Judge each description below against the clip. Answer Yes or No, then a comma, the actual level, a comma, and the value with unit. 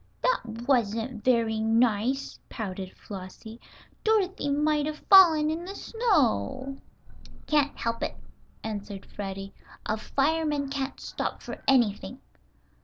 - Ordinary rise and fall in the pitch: No, wide, 5.7 semitones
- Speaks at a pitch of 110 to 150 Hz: No, very high, 255 Hz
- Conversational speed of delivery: No, slow, 110 wpm